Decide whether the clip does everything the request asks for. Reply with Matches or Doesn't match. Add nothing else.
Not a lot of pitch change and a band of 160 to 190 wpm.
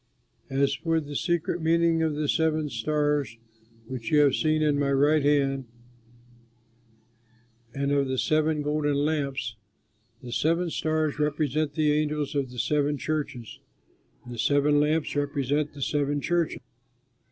Doesn't match